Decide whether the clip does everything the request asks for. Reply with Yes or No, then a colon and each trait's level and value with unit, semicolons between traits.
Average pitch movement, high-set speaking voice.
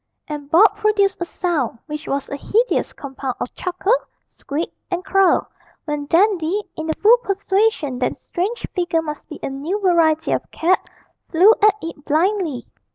Yes: average, 4.9 semitones; very high, 345 Hz